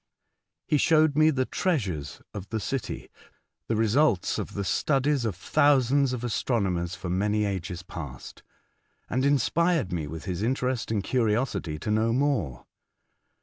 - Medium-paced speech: Yes, average, 150 wpm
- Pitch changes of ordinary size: No, wide, 6.7 semitones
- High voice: No, low, 115 Hz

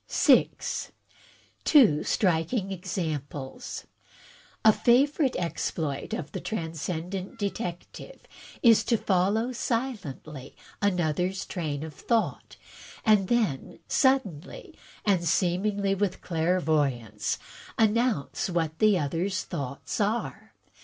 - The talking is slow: Yes, slow, 90 wpm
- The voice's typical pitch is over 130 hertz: Yes, medium, 185 Hz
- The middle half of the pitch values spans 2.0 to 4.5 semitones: No, wide, 5.6 semitones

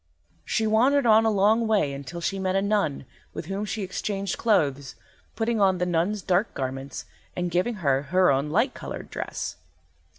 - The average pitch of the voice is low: No, high, 190 Hz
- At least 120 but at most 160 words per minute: No, average, 175 wpm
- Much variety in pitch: Yes, wide, 5.7 semitones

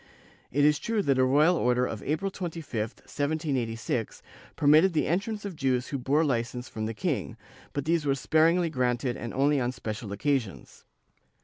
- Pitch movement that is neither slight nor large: Yes, average, 4.4 semitones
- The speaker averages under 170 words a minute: No, average, 175 wpm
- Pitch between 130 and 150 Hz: Yes, medium, 140 Hz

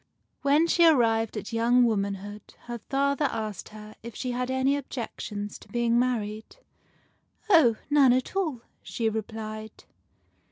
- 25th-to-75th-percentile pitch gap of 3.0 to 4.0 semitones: Yes, average, 3.7 semitones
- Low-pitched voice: No, high, 235 Hz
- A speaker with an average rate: Yes, average, 150 wpm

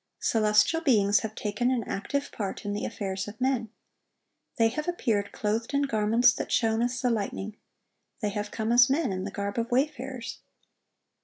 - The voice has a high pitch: Yes, high, 225 Hz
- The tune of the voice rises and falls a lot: No, average, 3.3 semitones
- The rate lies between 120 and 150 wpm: No, average, 175 wpm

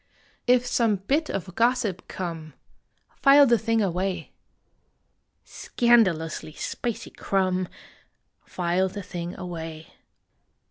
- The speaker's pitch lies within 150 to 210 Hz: Yes, high, 190 Hz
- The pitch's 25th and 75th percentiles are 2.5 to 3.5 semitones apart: No, average, 5.0 semitones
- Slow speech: Yes, slow, 95 wpm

